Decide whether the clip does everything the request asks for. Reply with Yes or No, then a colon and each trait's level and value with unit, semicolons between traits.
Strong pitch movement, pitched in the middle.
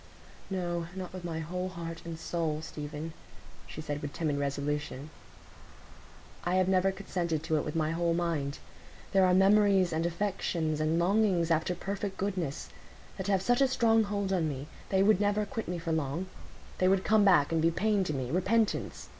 No: average, 3.5 semitones; medium, 175 Hz